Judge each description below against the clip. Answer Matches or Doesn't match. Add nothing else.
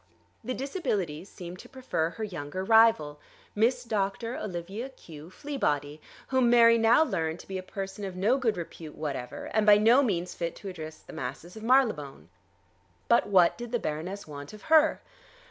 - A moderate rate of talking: Matches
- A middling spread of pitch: Doesn't match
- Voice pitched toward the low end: Doesn't match